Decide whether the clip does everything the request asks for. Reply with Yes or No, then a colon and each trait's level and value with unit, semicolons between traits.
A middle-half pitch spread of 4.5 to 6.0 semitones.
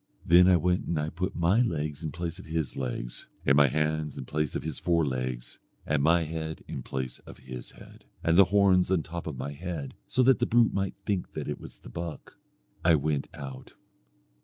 No: average, 3.9 semitones